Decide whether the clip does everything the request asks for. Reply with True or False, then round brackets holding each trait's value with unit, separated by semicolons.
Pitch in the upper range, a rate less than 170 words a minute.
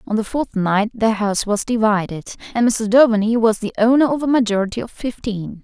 False (220 Hz; 200 wpm)